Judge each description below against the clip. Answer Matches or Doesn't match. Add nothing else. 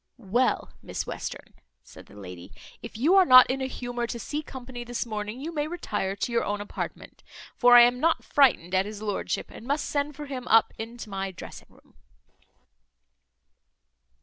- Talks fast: Doesn't match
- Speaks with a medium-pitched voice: Doesn't match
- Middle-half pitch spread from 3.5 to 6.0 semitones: Matches